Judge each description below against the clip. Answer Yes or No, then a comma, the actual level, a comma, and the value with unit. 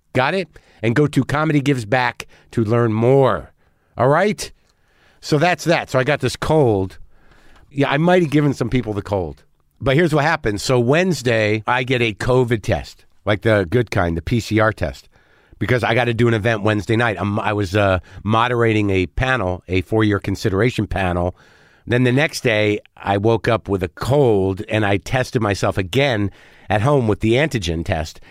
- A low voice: Yes, low, 115 Hz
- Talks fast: No, average, 190 wpm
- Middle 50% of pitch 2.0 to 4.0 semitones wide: No, average, 4.5 semitones